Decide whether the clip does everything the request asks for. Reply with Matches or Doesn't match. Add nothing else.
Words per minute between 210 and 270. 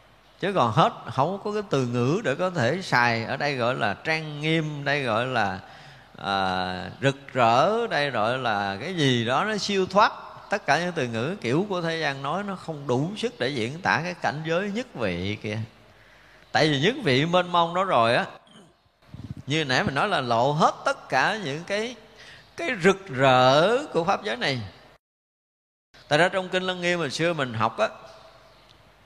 Doesn't match